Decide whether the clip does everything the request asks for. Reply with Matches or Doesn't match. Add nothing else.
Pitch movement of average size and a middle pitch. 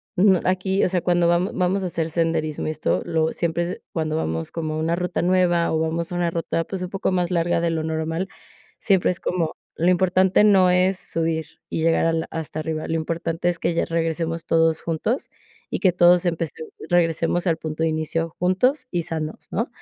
Doesn't match